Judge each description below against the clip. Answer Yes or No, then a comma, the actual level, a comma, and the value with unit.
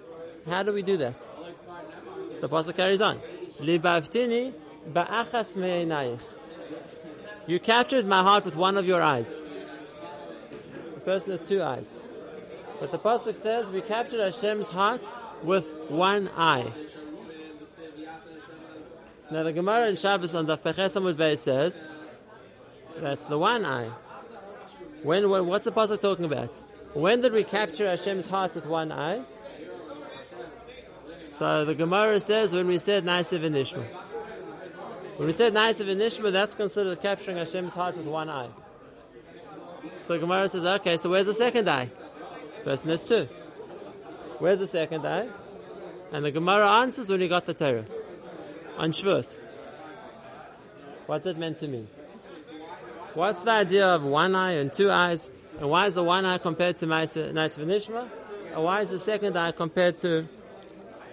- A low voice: No, medium, 180 Hz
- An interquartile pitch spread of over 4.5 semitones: No, average, 4.1 semitones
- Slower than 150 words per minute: Yes, average, 140 wpm